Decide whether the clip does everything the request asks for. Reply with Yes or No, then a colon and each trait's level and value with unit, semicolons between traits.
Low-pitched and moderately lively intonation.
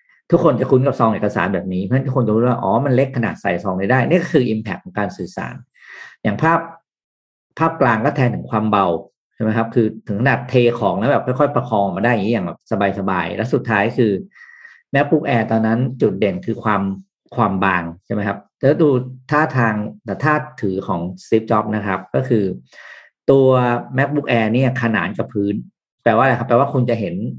Yes: low, 115 Hz; average, 4.6 semitones